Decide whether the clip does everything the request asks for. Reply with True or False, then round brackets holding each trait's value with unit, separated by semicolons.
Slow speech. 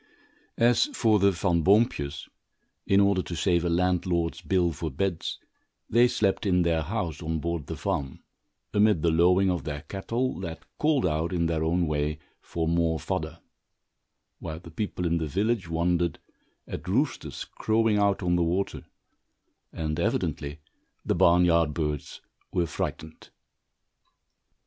False (150 wpm)